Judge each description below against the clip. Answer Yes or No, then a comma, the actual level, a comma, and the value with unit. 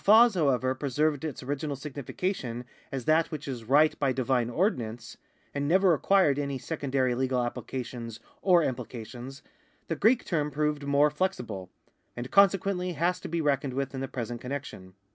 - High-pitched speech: No, medium, 140 Hz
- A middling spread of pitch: Yes, average, 4.0 semitones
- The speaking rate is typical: Yes, average, 170 wpm